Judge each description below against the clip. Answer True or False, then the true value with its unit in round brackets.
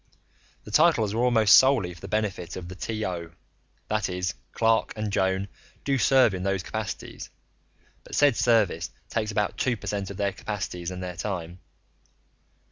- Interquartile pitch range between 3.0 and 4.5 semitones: True (3.5 semitones)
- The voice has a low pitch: True (100 Hz)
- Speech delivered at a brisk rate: False (165 wpm)